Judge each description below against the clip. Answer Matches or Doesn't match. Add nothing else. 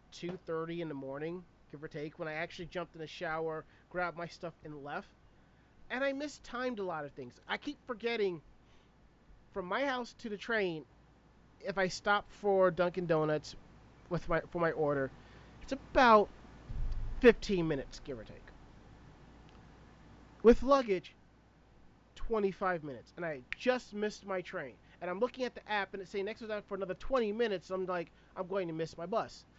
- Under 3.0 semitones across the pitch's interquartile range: Doesn't match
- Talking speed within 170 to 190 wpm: Matches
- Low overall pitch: Doesn't match